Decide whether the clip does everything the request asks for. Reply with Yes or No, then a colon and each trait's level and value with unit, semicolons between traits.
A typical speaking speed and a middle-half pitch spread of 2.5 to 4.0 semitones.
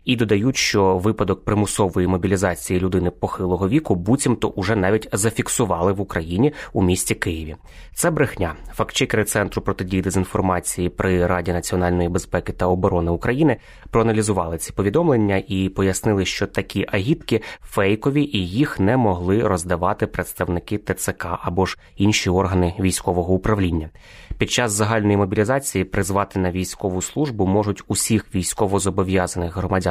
Yes: average, 130 wpm; average, 3.0 semitones